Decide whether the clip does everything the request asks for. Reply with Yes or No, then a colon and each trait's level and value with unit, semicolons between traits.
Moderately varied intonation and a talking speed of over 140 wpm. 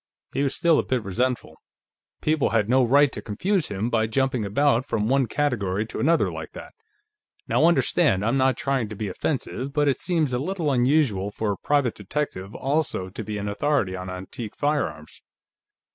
No: wide, 5.7 semitones; average, 185 wpm